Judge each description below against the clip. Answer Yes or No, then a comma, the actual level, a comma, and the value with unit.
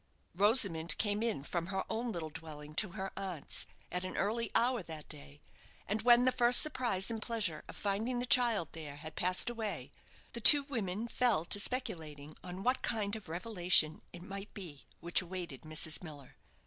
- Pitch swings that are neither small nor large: No, wide, 6.0 semitones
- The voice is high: Yes, high, 195 Hz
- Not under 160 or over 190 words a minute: Yes, average, 180 wpm